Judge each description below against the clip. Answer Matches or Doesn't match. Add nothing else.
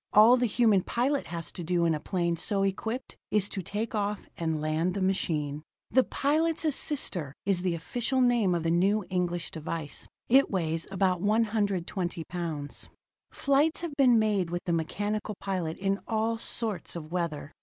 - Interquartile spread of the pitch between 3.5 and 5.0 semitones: Matches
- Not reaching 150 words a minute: Doesn't match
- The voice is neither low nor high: Doesn't match